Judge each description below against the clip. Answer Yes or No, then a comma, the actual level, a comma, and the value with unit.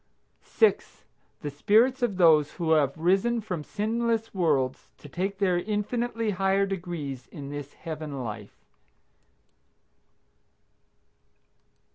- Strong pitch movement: Yes, wide, 6.1 semitones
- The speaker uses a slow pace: Yes, slow, 105 wpm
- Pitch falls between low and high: Yes, medium, 180 Hz